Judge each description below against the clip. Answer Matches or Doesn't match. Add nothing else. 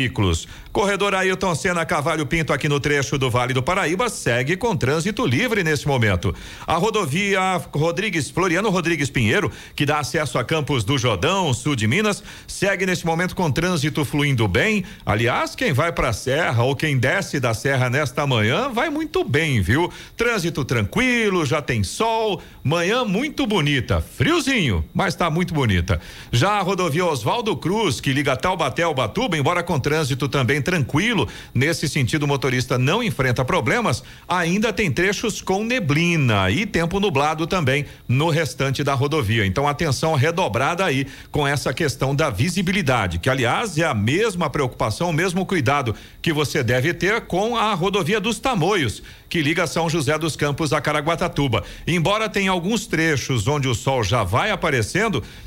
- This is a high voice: Doesn't match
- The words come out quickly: Doesn't match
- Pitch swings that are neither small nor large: Doesn't match